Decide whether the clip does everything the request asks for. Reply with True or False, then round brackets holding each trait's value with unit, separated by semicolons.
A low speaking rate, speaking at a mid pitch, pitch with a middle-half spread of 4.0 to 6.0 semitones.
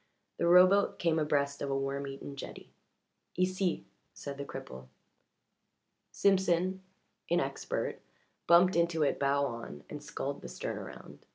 True (130 wpm; 155 Hz; 4.6 semitones)